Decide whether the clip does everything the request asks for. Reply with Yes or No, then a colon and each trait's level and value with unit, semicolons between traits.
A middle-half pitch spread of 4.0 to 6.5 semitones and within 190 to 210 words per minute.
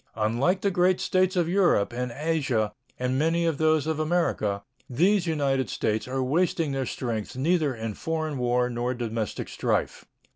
No: wide, 5.4 semitones; average, 160 wpm